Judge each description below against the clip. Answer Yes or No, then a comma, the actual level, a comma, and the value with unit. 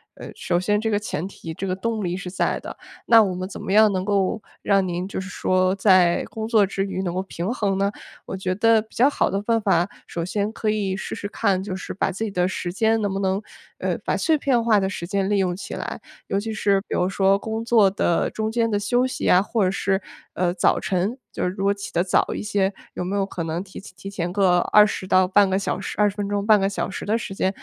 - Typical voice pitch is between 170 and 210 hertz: Yes, high, 195 Hz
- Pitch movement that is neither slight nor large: No, narrow, 2.2 semitones